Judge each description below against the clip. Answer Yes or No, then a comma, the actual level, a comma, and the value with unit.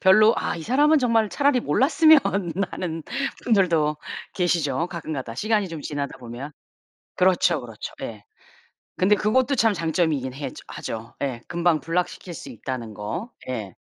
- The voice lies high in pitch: No, medium, 170 Hz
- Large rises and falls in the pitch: Yes, wide, 8.0 semitones